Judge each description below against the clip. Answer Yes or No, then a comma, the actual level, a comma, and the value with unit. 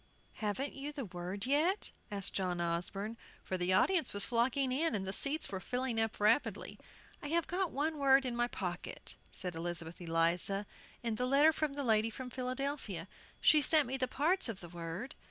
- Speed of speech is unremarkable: Yes, average, 190 wpm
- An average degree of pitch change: No, wide, 6.8 semitones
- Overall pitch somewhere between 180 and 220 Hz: No, high, 235 Hz